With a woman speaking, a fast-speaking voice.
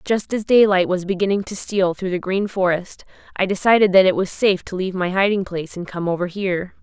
Yes: female; fast, 230 wpm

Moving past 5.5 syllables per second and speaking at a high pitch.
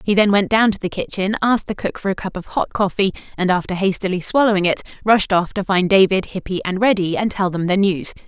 Yes: 6.0 syllables/s; high, 195 Hz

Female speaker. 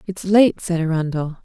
Yes: female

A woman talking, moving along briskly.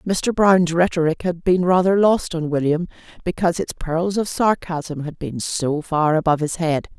No: female; average, 180 wpm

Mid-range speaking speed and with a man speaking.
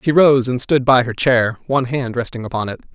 No: fast, 245 wpm; male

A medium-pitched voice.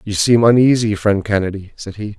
No: low, 105 Hz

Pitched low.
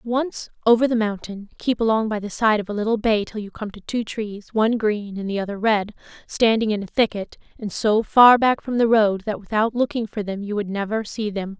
No: high, 215 Hz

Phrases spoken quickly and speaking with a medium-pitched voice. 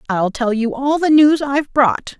No: fast, 220 wpm; very high, 265 Hz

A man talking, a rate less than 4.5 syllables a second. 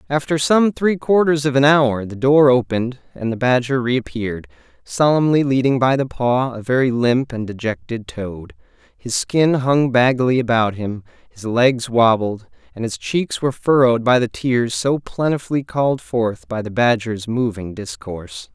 No: male; 4.7 syllables/s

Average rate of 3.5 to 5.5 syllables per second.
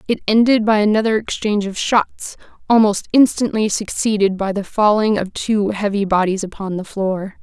Yes: 5.0 syllables/s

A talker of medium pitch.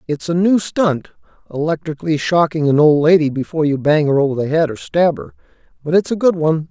Yes: medium, 160 Hz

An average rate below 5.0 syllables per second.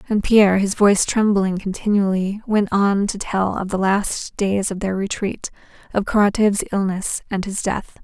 Yes: 4.6 syllables/s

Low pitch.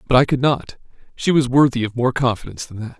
Yes: low, 125 Hz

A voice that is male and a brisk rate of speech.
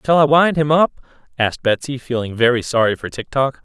Yes: male; fast, 215 wpm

